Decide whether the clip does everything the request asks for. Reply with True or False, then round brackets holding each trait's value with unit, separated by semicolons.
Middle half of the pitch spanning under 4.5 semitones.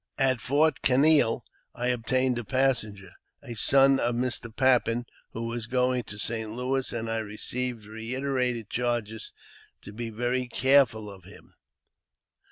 True (2.5 semitones)